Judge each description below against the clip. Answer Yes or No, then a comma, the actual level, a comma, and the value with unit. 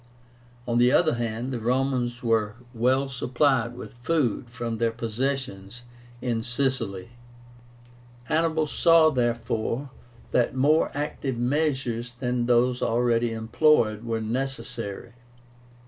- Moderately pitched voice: No, low, 120 Hz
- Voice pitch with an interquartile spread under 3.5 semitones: Yes, narrow, 2.5 semitones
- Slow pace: Yes, slow, 110 wpm